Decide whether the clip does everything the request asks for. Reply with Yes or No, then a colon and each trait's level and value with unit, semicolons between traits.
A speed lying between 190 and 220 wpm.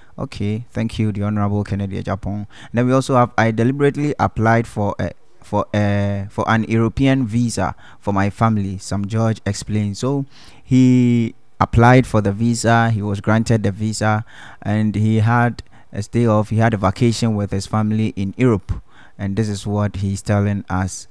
No: average, 175 wpm